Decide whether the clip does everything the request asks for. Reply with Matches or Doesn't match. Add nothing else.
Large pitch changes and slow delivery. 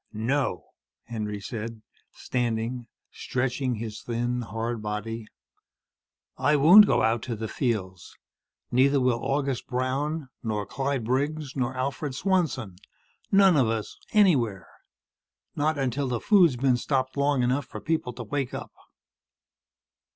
Doesn't match